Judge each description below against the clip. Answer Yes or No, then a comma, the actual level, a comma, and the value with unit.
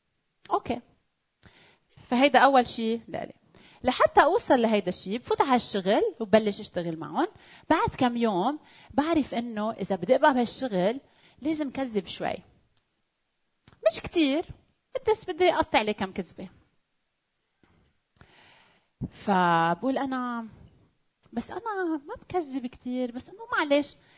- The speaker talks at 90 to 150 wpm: Yes, average, 110 wpm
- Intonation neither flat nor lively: No, wide, 6.4 semitones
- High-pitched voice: Yes, very high, 255 Hz